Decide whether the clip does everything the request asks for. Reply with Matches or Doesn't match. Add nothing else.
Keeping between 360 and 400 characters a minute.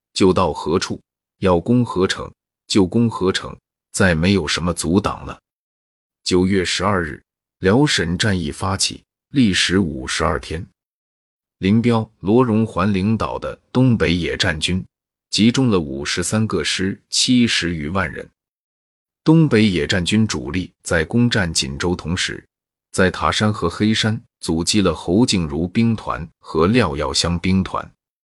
Doesn't match